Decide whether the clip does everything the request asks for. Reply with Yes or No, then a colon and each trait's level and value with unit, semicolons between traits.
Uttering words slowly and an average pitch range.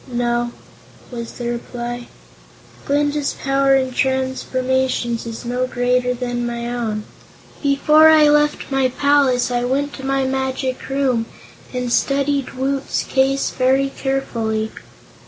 No: slow, 120 wpm; narrow, 2.1 semitones